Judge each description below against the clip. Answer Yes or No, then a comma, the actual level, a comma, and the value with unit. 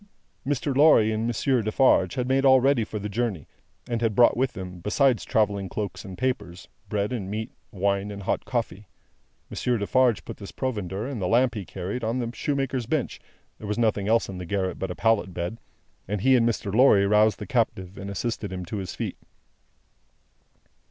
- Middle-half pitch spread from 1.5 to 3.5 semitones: No, average, 3.9 semitones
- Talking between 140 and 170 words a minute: No, average, 195 wpm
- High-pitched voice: No, low, 110 Hz